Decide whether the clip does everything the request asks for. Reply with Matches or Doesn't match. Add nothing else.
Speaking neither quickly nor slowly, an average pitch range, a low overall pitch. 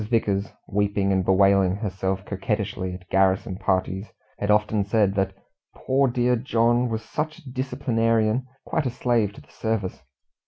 Matches